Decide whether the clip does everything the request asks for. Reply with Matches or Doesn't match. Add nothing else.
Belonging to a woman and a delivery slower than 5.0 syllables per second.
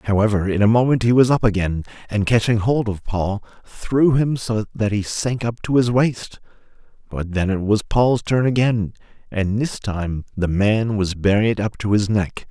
Doesn't match